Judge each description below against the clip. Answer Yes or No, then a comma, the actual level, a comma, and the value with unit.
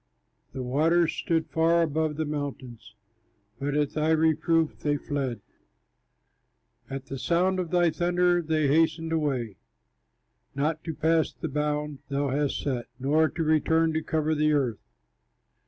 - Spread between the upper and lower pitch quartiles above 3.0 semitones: No, narrow, 2.4 semitones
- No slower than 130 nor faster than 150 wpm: Yes, average, 140 wpm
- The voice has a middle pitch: Yes, medium, 155 Hz